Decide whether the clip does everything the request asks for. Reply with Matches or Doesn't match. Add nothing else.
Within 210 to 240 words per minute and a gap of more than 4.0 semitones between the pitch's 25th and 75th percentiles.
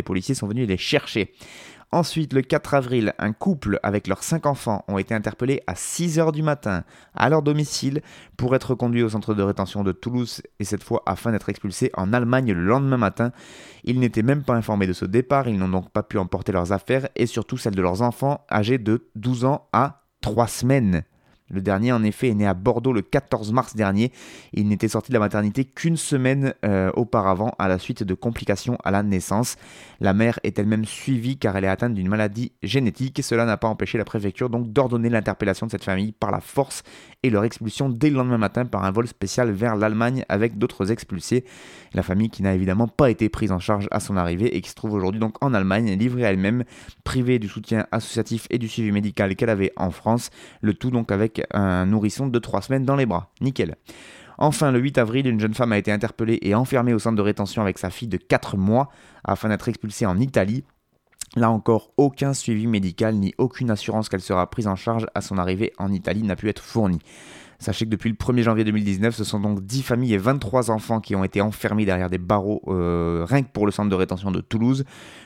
Doesn't match